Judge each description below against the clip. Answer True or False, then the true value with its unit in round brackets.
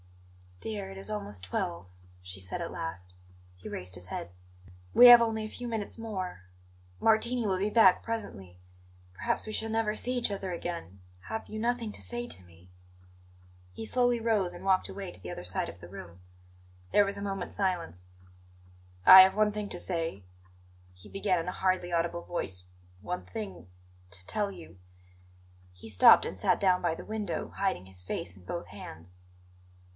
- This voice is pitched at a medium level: True (175 Hz)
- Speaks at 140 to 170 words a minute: False (180 wpm)